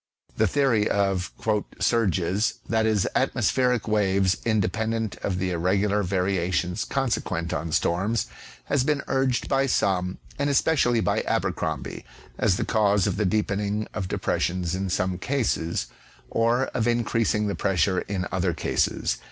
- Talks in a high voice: No, low, 105 Hz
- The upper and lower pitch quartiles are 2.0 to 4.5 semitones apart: Yes, average, 3.7 semitones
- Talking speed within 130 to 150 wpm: Yes, average, 145 wpm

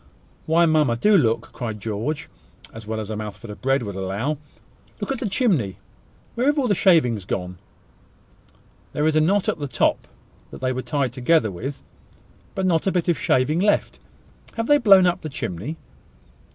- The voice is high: No, medium, 140 Hz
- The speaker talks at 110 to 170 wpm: No, average, 185 wpm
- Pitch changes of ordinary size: No, wide, 8.0 semitones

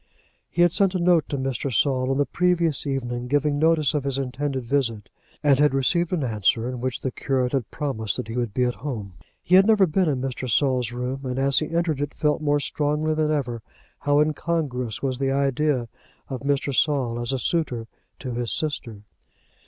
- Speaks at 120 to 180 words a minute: No, fast, 205 wpm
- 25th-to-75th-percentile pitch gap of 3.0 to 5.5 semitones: Yes, average, 3.3 semitones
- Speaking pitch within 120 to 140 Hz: Yes, low, 135 Hz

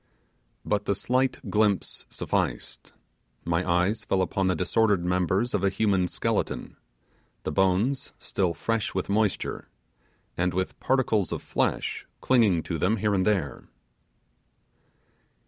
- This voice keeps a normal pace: No, slow, 130 wpm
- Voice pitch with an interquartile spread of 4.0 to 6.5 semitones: No, average, 3.2 semitones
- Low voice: Yes, very low, 95 Hz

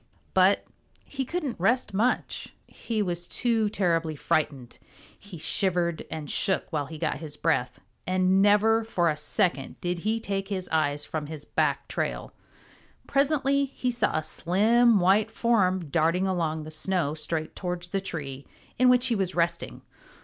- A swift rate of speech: No, average, 155 wpm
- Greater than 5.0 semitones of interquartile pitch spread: Yes, wide, 5.4 semitones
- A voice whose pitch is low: No, medium, 185 Hz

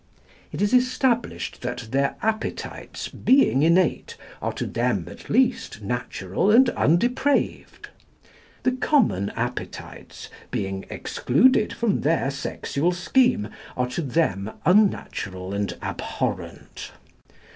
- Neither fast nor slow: No, slow, 105 wpm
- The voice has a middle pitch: Yes, medium, 165 Hz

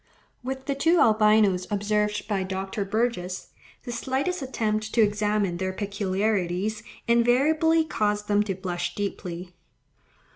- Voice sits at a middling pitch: No, high, 210 Hz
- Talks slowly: Yes, slow, 120 wpm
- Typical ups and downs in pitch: Yes, average, 3.5 semitones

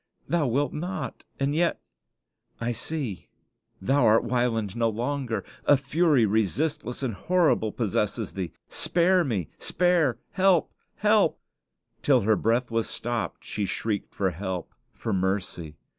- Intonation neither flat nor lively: No, wide, 5.7 semitones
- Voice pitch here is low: Yes, low, 120 Hz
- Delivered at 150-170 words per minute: No, slow, 135 wpm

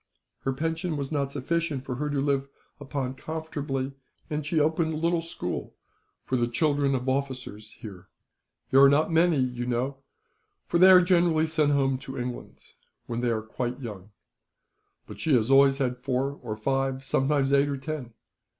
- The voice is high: No, low, 135 Hz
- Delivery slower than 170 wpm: No, average, 175 wpm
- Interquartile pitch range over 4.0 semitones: No, average, 3.3 semitones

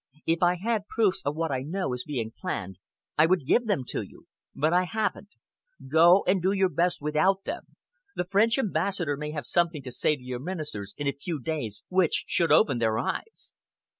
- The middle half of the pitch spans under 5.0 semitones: No, average, 5.3 semitones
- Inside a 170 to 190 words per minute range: No, average, 200 wpm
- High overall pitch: No, medium, 165 Hz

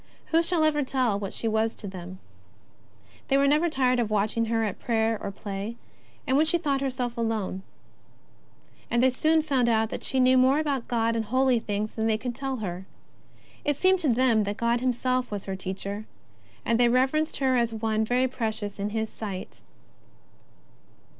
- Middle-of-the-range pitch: No, high, 235 Hz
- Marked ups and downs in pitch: No, average, 3.4 semitones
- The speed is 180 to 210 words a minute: Yes, average, 185 wpm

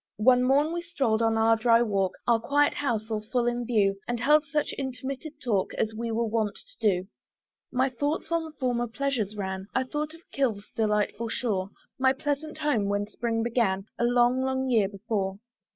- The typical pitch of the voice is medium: No, high, 240 Hz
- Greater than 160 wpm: Yes, average, 185 wpm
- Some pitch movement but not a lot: Yes, average, 4.0 semitones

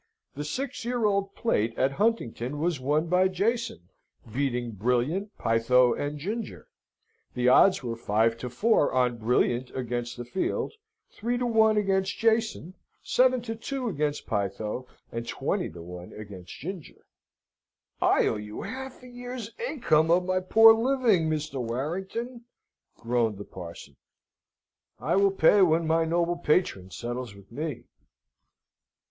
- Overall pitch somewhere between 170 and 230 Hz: No, medium, 160 Hz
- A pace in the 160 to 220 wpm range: No, average, 140 wpm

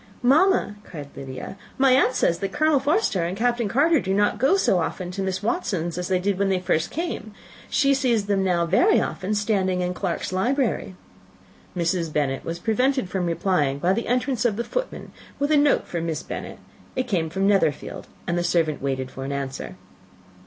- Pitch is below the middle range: No, high, 195 Hz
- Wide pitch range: Yes, wide, 6.7 semitones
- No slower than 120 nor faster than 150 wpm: No, average, 190 wpm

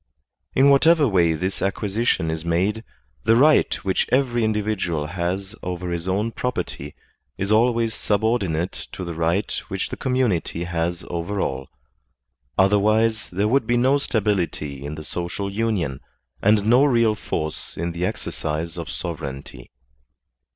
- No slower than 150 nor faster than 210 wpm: No, average, 140 wpm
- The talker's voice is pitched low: Yes, very low, 95 Hz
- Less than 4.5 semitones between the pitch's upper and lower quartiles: No, average, 5.0 semitones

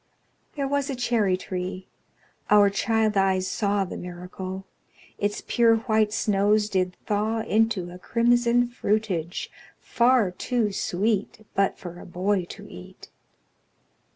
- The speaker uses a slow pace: Yes, slow, 125 wpm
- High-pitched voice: Yes, high, 205 Hz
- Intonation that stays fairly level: No, average, 3.4 semitones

